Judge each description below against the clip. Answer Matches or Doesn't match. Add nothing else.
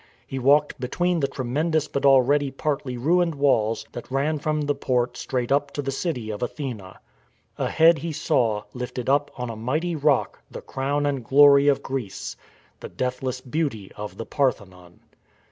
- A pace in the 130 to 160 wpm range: Doesn't match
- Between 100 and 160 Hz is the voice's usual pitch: Matches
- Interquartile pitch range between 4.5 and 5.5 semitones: Doesn't match